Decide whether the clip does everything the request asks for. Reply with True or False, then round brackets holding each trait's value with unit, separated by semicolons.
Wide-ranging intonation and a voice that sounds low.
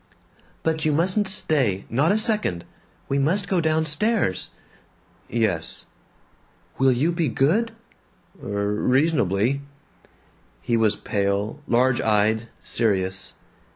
True (7.7 semitones; 130 Hz)